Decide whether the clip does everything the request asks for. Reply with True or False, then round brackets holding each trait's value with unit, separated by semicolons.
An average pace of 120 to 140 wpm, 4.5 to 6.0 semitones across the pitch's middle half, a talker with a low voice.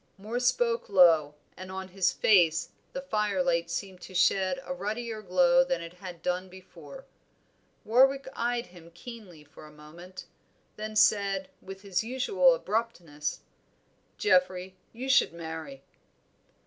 False (135 wpm; 5.2 semitones; 195 Hz)